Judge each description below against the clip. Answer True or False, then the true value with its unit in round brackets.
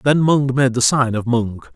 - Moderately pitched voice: False (125 Hz)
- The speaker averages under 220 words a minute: False (240 wpm)